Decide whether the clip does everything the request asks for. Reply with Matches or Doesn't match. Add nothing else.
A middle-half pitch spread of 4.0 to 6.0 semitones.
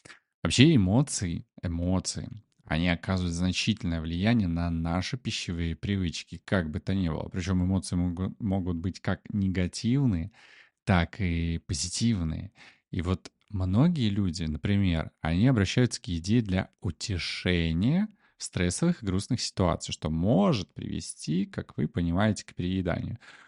Matches